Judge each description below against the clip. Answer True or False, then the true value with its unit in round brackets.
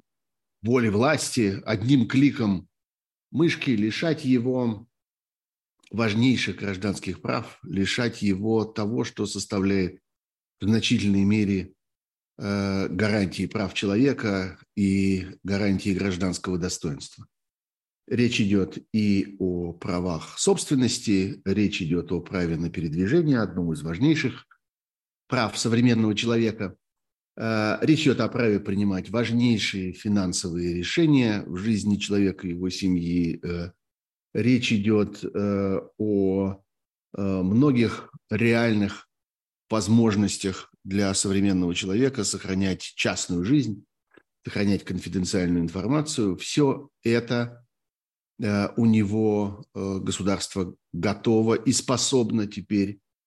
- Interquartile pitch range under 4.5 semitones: True (3.3 semitones)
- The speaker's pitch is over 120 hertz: False (100 Hz)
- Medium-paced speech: False (90 wpm)